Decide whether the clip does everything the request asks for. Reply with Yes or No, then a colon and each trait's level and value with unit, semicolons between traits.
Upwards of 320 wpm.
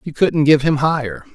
No: fast, 225 wpm